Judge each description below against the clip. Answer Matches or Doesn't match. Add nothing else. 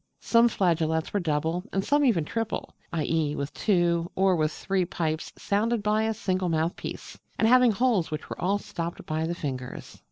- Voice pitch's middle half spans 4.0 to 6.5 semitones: Matches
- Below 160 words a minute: Doesn't match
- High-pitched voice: Doesn't match